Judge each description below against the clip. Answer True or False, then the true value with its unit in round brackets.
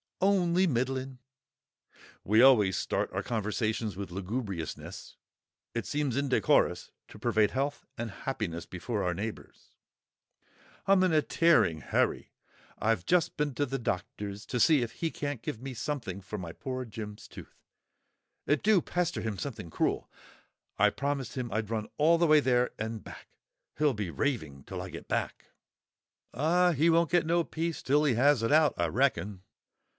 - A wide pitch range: True (6.0 semitones)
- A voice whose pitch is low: True (125 Hz)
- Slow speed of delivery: False (160 wpm)